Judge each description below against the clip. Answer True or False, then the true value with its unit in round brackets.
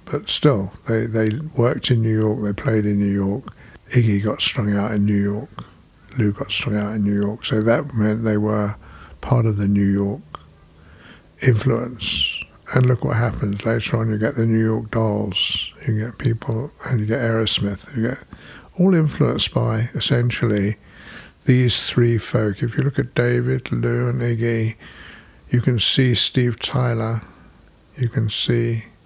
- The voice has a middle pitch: False (115 Hz)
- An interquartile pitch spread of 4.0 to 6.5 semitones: False (2.9 semitones)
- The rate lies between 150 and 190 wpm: True (170 wpm)